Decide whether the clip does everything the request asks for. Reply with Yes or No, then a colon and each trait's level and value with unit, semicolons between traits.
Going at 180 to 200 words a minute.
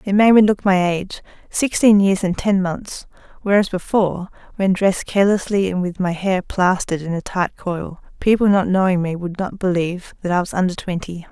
Yes: average, 185 wpm